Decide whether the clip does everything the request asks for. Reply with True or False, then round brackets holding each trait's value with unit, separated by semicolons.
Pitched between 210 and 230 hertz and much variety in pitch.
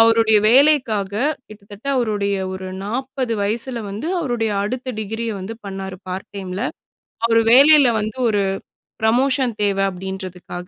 False (220 Hz; 3.9 semitones)